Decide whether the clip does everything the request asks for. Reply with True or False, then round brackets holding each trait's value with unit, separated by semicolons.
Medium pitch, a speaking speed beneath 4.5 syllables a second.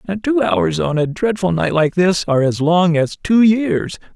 True (170 Hz; 4.3 syllables/s)